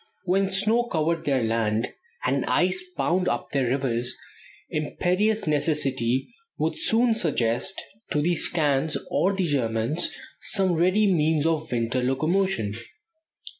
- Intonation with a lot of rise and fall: Yes, wide, 6.3 semitones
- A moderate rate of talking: No, slow, 125 wpm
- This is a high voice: No, medium, 155 Hz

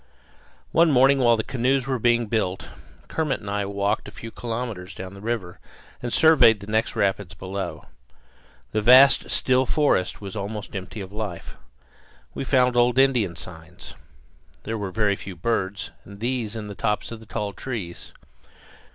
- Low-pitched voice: Yes, low, 110 Hz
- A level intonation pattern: No, average, 3.8 semitones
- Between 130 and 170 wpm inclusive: Yes, average, 165 wpm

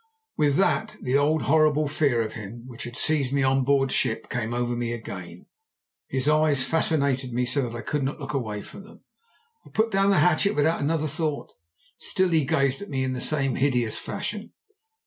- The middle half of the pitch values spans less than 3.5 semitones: No, average, 4.0 semitones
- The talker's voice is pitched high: No, medium, 140 Hz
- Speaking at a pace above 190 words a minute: Yes, average, 200 wpm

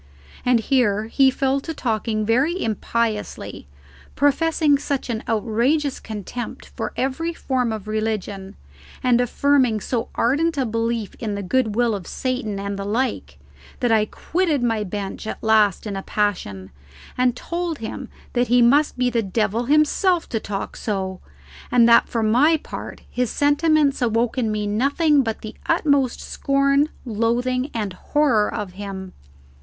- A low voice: No, high, 235 Hz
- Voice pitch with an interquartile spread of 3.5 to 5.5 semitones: Yes, average, 4.4 semitones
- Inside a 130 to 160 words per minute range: Yes, average, 150 wpm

